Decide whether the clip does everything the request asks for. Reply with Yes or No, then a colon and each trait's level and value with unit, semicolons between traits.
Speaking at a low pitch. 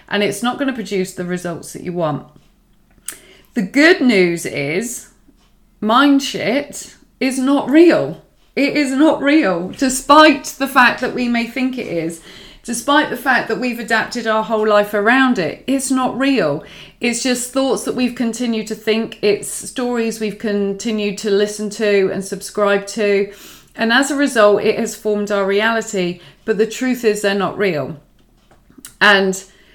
No: high, 220 Hz